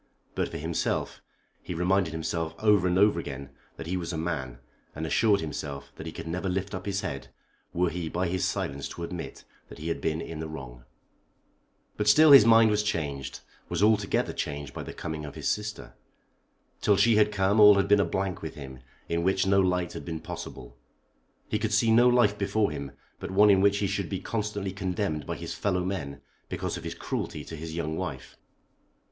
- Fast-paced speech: Yes, fast, 210 wpm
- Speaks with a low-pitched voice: Yes, very low, 90 Hz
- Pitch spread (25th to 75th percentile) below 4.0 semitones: No, average, 4.5 semitones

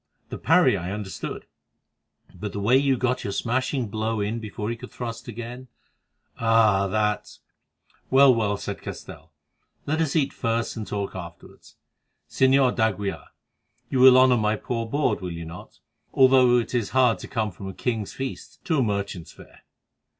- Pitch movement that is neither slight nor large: Yes, average, 3.8 semitones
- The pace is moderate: Yes, average, 165 wpm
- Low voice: Yes, low, 115 Hz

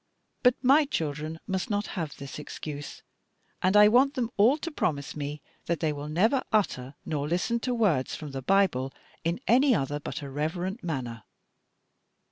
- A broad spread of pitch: Yes, wide, 7.3 semitones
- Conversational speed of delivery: Yes, average, 170 wpm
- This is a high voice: No, medium, 170 Hz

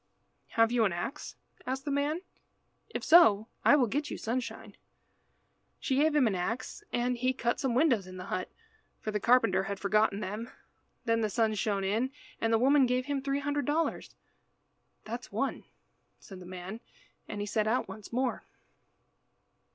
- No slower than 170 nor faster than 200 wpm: Yes, average, 175 wpm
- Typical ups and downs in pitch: Yes, average, 4.3 semitones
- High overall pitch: Yes, high, 230 Hz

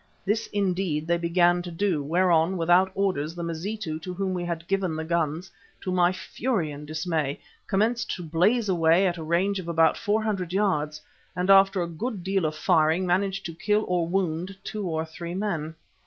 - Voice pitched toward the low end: No, medium, 175 Hz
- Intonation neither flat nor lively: Yes, average, 3.0 semitones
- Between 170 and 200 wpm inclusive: Yes, average, 190 wpm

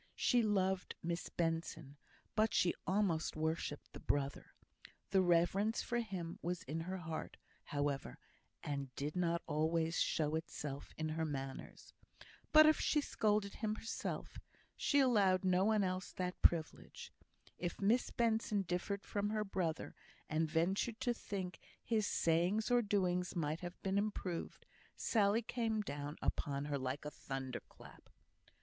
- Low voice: No, medium, 180 Hz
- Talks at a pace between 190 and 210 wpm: No, average, 145 wpm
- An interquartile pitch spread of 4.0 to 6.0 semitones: Yes, average, 4.8 semitones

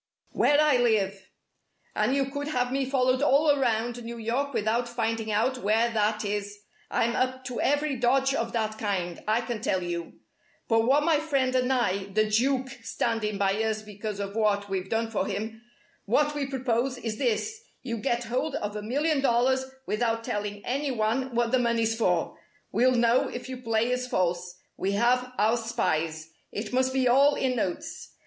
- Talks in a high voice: Yes, high, 235 Hz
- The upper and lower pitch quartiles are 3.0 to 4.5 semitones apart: Yes, average, 3.4 semitones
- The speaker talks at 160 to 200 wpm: Yes, average, 185 wpm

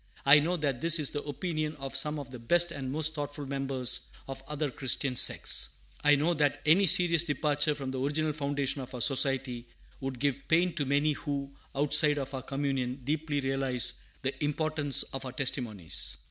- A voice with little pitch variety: Yes, narrow, 2.2 semitones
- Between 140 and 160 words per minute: No, average, 185 wpm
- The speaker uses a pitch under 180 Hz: Yes, medium, 140 Hz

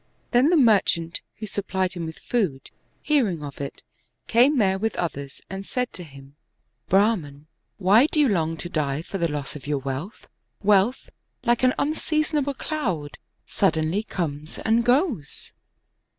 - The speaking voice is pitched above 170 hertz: Yes, high, 190 Hz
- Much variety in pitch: Yes, wide, 7.8 semitones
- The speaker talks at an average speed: Yes, average, 155 wpm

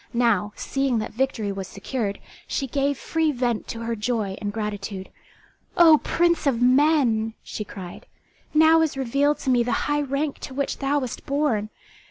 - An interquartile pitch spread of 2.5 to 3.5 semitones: No, average, 4.7 semitones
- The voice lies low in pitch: No, very high, 250 Hz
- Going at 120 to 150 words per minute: No, average, 170 wpm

